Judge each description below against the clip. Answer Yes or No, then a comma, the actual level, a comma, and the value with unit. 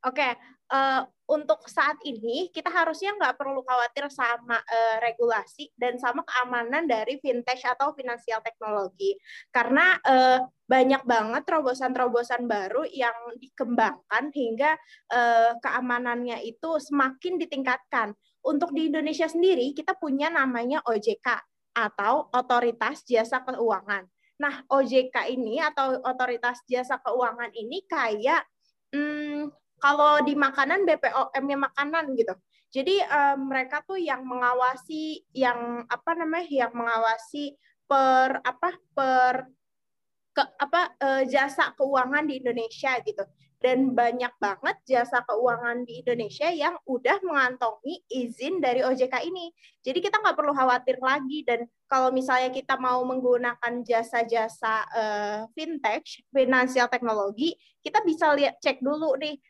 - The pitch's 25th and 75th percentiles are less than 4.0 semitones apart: Yes, average, 3.6 semitones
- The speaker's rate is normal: Yes, average, 125 wpm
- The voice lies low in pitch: No, very high, 260 Hz